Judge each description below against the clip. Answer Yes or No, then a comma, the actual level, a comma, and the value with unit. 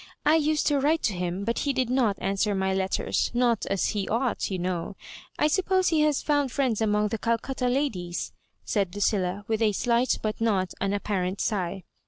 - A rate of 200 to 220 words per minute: Yes, fast, 205 wpm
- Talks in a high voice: Yes, high, 220 Hz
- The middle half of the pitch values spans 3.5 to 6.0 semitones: Yes, average, 5.3 semitones